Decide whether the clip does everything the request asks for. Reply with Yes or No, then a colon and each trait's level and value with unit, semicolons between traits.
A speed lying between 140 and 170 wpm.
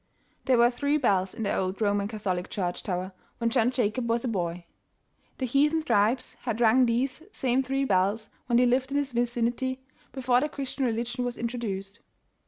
No: average, 185 wpm